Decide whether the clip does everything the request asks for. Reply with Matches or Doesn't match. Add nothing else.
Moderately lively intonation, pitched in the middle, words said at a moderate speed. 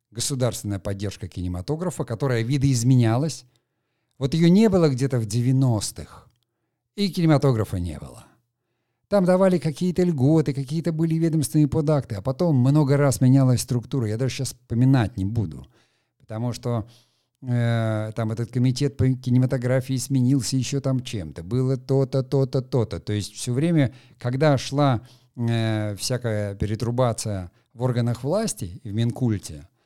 Doesn't match